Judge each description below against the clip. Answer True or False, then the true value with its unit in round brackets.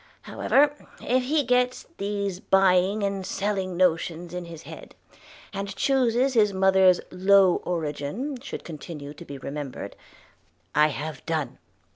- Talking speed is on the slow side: True (130 wpm)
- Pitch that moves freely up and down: False (4.3 semitones)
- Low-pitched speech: False (190 Hz)